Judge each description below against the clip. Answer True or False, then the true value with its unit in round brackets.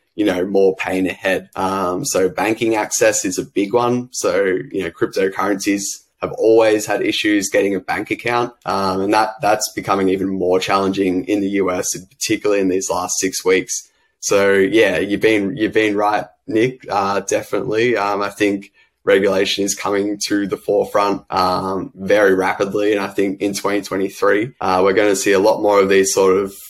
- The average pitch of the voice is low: True (100 Hz)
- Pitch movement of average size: False (2.0 semitones)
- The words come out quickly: False (185 wpm)